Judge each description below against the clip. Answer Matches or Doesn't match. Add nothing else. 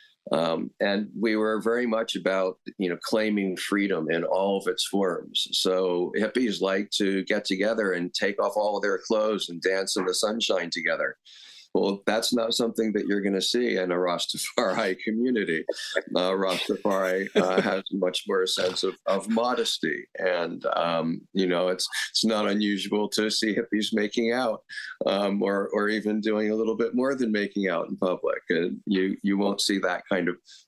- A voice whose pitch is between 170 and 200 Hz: Doesn't match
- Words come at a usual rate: Matches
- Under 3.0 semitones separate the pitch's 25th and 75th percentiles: Matches